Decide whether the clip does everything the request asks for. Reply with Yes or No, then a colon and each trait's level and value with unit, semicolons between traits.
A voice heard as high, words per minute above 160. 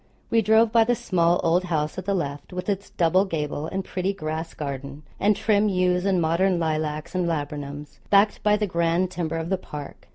No: medium, 175 Hz; average, 200 wpm